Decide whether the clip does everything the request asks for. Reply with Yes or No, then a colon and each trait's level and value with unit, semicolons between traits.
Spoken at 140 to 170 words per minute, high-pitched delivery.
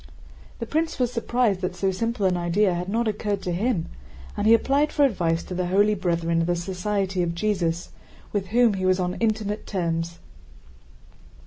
No: average, 185 wpm; high, 195 Hz